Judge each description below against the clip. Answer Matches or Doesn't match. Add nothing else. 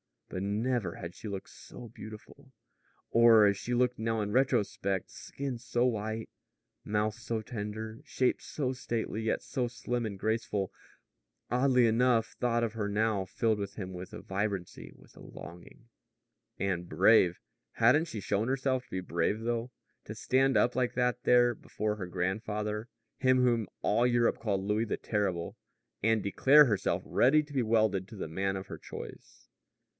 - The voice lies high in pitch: Doesn't match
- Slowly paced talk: Doesn't match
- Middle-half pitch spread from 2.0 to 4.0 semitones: Matches